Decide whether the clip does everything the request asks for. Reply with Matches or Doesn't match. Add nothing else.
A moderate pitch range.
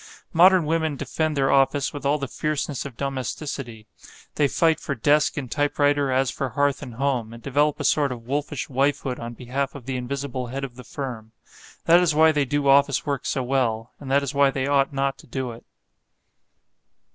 Doesn't match